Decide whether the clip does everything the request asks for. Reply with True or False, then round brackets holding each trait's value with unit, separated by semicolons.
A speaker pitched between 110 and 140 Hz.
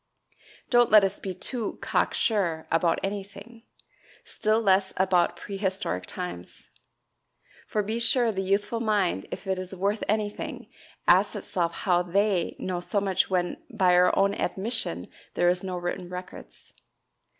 False (190 Hz)